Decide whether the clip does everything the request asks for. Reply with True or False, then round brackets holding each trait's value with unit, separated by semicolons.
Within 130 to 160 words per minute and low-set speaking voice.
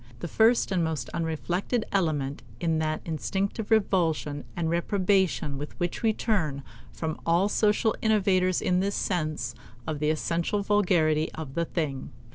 False (145 wpm; 170 Hz)